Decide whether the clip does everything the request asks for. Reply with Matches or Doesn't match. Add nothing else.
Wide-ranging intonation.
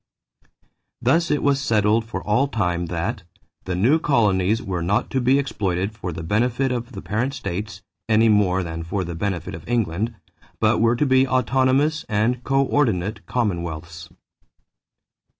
Matches